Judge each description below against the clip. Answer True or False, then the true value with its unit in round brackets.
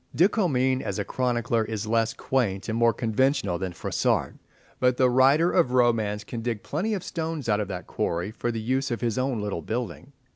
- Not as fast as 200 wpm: False (205 wpm)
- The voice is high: False (120 Hz)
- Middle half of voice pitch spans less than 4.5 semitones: True (3.5 semitones)